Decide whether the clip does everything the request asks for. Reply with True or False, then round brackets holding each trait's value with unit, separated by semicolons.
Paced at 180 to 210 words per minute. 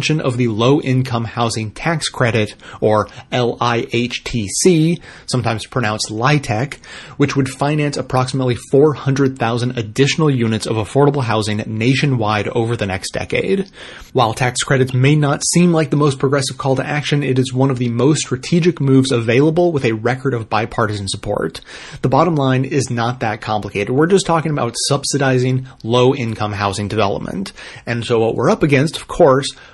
False (160 wpm)